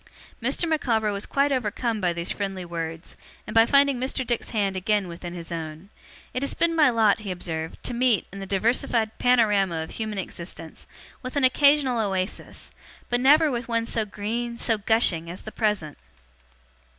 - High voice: Yes, high, 215 Hz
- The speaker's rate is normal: Yes, average, 175 wpm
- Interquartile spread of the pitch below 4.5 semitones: No, average, 5.0 semitones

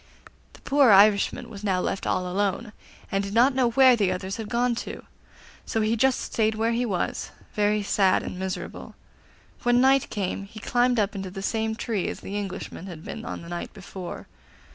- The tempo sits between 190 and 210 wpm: Yes, average, 195 wpm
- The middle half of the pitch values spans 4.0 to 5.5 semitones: No, average, 3.5 semitones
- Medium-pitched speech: No, high, 210 Hz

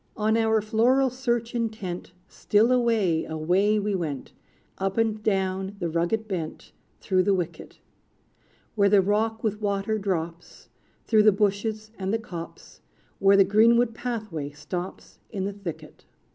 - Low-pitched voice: No, high, 205 Hz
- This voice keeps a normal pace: Yes, average, 145 wpm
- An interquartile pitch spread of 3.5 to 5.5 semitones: No, average, 3.0 semitones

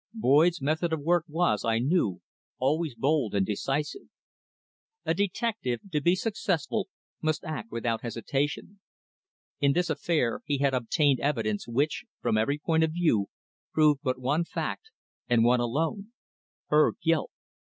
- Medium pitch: Yes, medium, 150 Hz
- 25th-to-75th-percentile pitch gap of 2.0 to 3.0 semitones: No, average, 5.3 semitones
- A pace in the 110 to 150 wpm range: Yes, average, 140 wpm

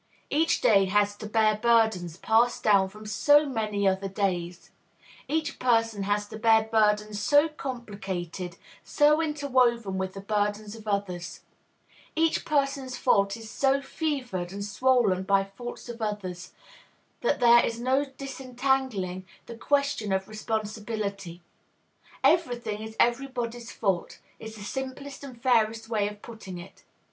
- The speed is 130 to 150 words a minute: Yes, average, 140 wpm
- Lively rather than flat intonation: No, average, 4.2 semitones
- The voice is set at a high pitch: Yes, high, 220 Hz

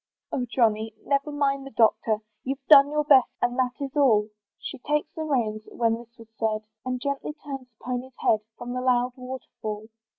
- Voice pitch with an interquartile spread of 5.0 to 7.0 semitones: No, average, 3.4 semitones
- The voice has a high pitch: Yes, very high, 250 Hz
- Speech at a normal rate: Yes, average, 195 wpm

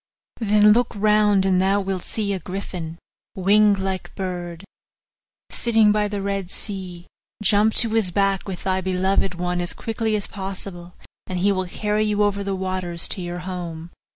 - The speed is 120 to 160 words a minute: No, average, 175 wpm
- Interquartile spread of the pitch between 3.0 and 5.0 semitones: No, narrow, 2.4 semitones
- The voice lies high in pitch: Yes, high, 195 Hz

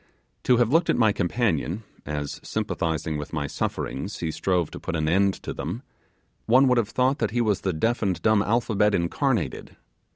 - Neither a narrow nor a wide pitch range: No, wide, 6.3 semitones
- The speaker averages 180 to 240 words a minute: Yes, average, 190 wpm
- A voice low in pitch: Yes, low, 100 Hz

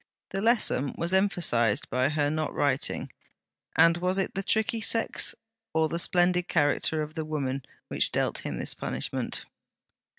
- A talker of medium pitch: Yes, medium, 160 Hz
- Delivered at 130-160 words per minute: Yes, average, 155 wpm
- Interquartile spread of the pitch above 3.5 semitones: Yes, average, 4.6 semitones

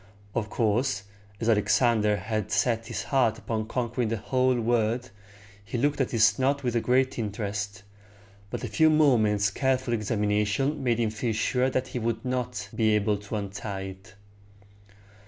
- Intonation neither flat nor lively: Yes, average, 3.2 semitones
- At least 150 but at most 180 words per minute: Yes, average, 155 wpm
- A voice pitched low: Yes, low, 115 Hz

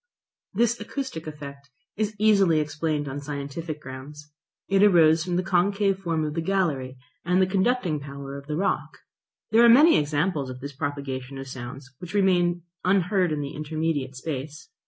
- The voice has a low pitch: No, medium, 155 Hz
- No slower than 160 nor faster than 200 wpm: Yes, average, 165 wpm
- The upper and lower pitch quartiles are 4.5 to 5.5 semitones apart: Yes, average, 5.2 semitones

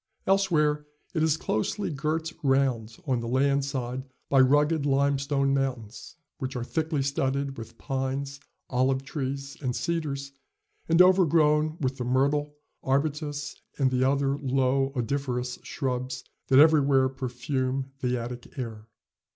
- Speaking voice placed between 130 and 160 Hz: Yes, low, 135 Hz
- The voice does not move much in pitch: Yes, narrow, 2.3 semitones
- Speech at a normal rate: No, slow, 130 wpm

